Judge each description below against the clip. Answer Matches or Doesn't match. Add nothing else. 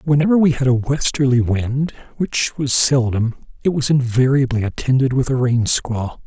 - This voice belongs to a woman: Doesn't match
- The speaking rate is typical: Matches